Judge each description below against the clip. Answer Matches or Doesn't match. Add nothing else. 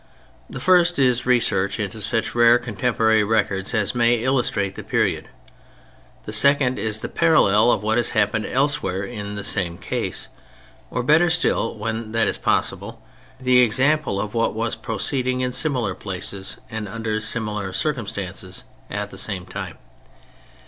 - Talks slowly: Doesn't match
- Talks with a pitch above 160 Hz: Doesn't match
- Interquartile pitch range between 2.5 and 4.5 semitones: Matches